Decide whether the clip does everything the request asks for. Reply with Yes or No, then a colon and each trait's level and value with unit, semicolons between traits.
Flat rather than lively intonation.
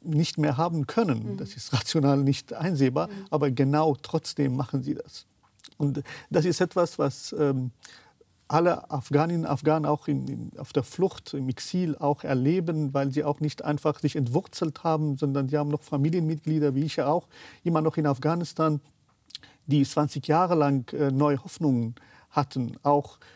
Yes: narrow, 2.3 semitones